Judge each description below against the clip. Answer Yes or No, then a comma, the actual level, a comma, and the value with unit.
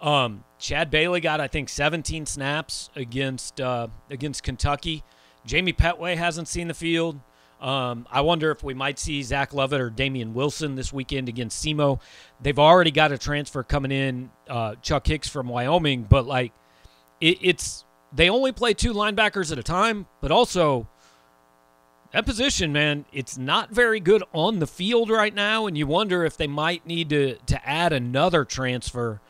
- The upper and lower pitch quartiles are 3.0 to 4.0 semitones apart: No, average, 4.9 semitones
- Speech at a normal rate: Yes, average, 170 wpm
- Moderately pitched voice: Yes, medium, 145 Hz